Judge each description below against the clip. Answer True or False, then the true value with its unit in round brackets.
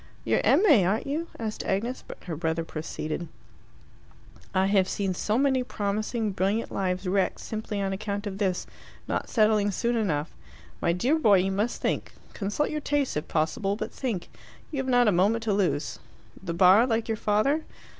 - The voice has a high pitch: True (205 Hz)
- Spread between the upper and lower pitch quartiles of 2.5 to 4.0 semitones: True (3.6 semitones)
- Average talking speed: True (175 wpm)